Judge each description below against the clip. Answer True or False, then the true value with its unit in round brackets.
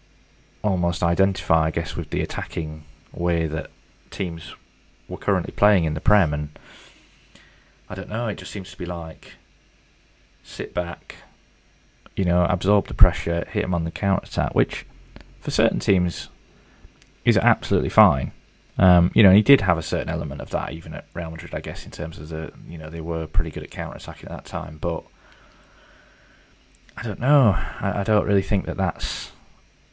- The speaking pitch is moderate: False (90 Hz)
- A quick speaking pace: False (180 wpm)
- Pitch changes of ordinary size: True (3.3 semitones)